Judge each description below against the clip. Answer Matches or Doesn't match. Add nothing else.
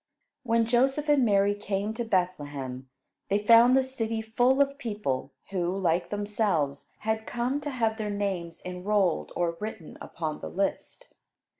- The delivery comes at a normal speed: Matches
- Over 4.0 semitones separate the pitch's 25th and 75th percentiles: Matches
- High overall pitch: Matches